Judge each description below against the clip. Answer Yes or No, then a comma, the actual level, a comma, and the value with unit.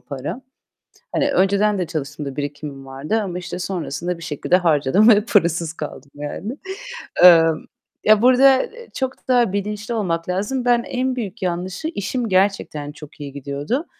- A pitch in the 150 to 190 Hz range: Yes, medium, 185 Hz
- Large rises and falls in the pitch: Yes, wide, 6.7 semitones